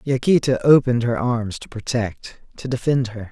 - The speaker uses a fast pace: No, average, 165 wpm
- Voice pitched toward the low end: Yes, low, 120 Hz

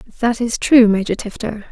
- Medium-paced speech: Yes, average, 175 wpm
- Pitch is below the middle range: No, high, 225 Hz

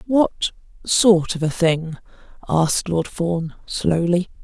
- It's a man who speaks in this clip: No, female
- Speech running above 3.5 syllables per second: No, 3.4 syllables/s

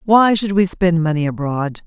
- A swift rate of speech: No, average, 195 wpm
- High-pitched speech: No, medium, 175 Hz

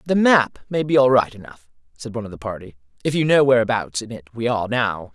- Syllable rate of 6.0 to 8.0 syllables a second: Yes, 6.3 syllables/s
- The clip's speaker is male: Yes, male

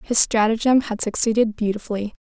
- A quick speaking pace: No, slow, 135 wpm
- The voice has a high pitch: Yes, high, 220 Hz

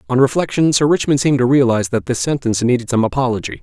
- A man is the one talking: Yes, male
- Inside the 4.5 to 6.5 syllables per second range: No, 7.3 syllables/s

